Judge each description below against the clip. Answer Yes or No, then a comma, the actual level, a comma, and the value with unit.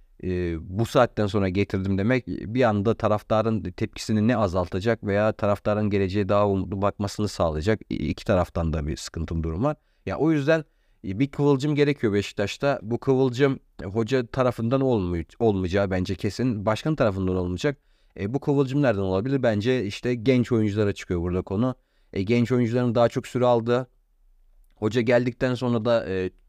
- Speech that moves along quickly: Yes, fast, 160 wpm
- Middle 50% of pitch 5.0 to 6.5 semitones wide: No, average, 4.6 semitones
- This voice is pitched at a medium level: No, low, 110 Hz